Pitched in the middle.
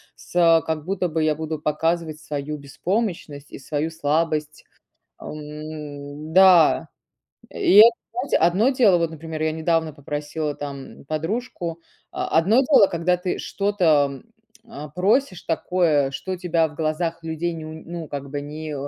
Yes: medium, 160 Hz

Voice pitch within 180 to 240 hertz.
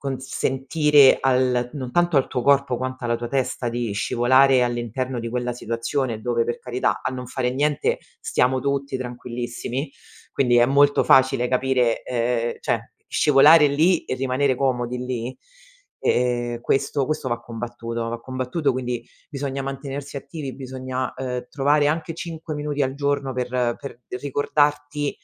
No: low, 130 Hz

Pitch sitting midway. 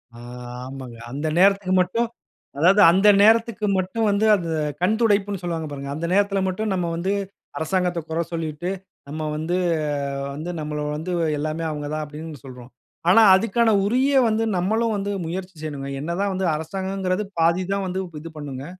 Yes: medium, 180 Hz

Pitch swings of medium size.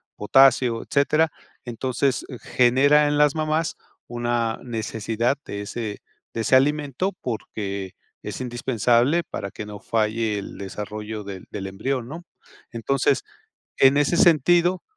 Yes: average, 4.7 semitones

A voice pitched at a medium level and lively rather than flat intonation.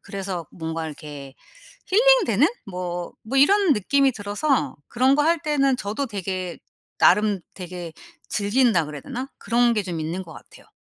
No: high, 205 Hz; wide, 7.3 semitones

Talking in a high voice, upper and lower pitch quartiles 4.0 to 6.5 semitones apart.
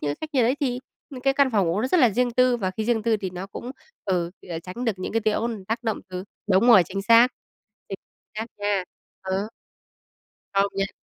Yes: high, 215 Hz; average, 4.3 semitones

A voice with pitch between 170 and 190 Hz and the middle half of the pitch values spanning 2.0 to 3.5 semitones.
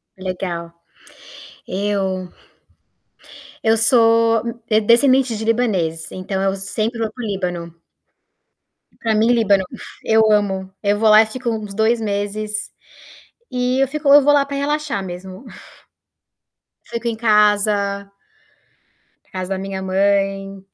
No: high, 210 Hz; average, 3.0 semitones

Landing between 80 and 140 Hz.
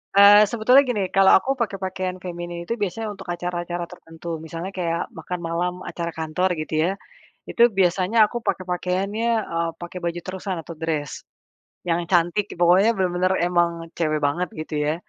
No: medium, 180 Hz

